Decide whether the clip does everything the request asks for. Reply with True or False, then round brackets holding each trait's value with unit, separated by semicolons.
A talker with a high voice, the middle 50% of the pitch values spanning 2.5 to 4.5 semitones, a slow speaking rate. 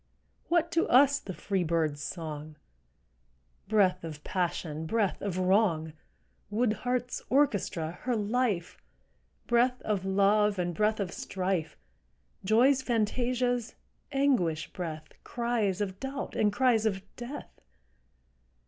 False (205 Hz; 5.5 semitones; 115 wpm)